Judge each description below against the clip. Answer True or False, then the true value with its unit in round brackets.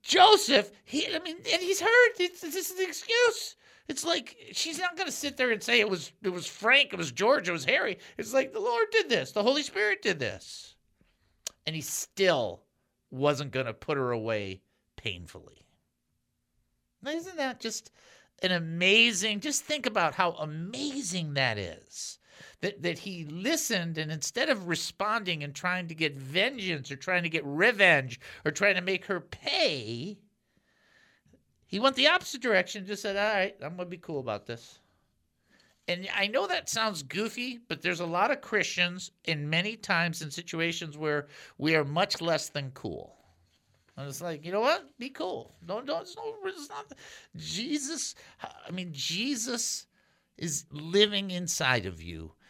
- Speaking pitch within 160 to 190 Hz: True (185 Hz)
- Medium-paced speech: True (175 wpm)